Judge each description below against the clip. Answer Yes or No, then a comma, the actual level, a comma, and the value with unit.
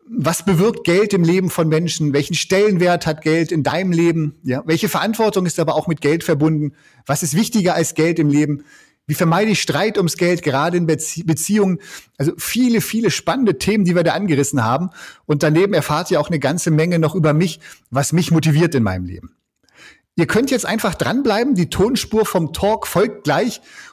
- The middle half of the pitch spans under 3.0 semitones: No, average, 4.1 semitones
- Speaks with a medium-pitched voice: Yes, medium, 170 Hz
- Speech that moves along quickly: Yes, fast, 195 wpm